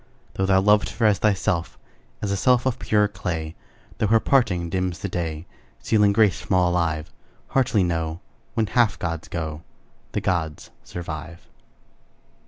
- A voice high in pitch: No, very low, 90 Hz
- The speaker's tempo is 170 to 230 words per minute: No, average, 155 wpm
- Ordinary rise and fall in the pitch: Yes, average, 4.0 semitones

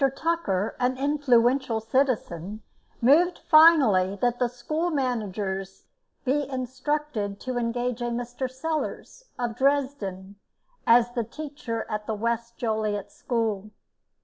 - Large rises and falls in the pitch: No, average, 4.3 semitones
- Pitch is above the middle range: Yes, high, 245 Hz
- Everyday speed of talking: No, slow, 110 wpm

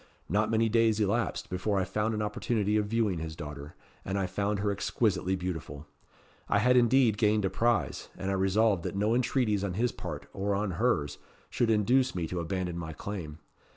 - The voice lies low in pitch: Yes, low, 100 Hz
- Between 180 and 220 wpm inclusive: Yes, average, 190 wpm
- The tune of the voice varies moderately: Yes, average, 3.3 semitones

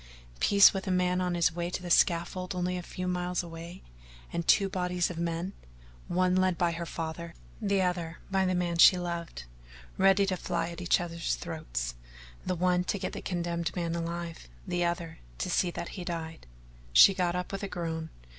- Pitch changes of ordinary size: No, narrow, 1.3 semitones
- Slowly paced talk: No, average, 195 wpm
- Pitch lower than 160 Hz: No, medium, 175 Hz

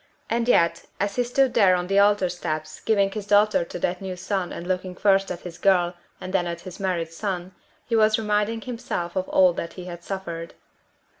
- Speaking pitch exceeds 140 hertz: Yes, medium, 185 Hz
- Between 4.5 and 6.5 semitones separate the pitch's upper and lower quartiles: No, average, 2.8 semitones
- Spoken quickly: Yes, fast, 210 wpm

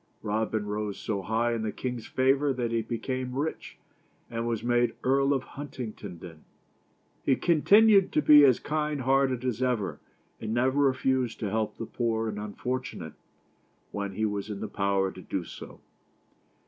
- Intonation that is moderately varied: Yes, average, 3.8 semitones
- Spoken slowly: No, average, 165 wpm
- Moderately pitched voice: No, low, 120 Hz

